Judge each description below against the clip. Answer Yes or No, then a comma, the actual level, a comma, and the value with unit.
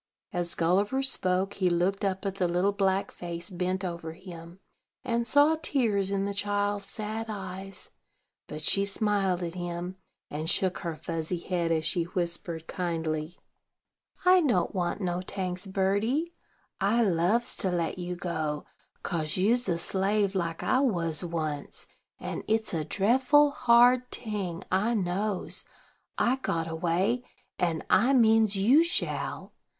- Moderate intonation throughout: Yes, average, 3.7 semitones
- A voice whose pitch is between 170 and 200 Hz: Yes, high, 190 Hz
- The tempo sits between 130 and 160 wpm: Yes, average, 145 wpm